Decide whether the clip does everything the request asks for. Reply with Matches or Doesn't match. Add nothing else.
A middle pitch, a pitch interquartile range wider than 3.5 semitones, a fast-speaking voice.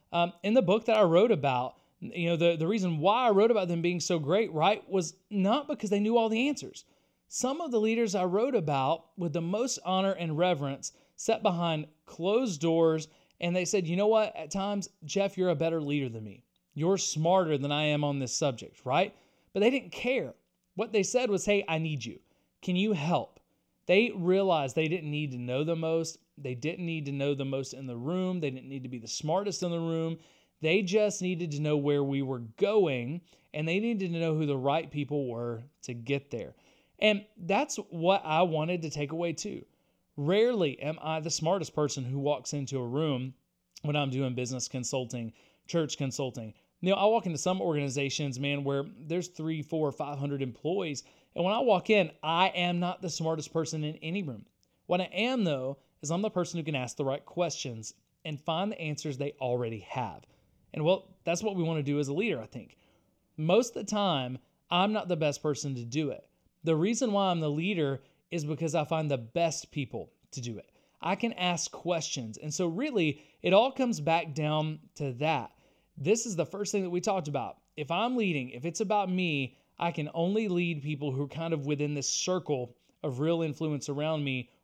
Matches